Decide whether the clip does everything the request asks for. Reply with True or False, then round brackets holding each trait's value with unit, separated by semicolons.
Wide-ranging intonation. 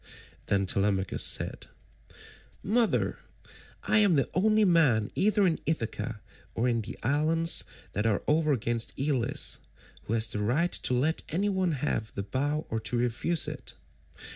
True (6.7 semitones)